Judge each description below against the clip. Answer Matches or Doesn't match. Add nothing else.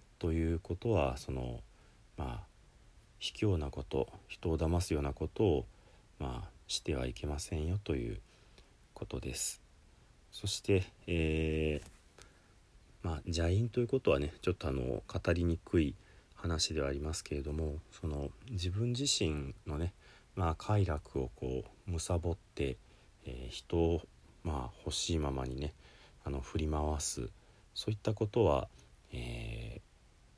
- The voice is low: Matches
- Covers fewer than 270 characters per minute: Matches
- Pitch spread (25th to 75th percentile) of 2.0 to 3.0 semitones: Doesn't match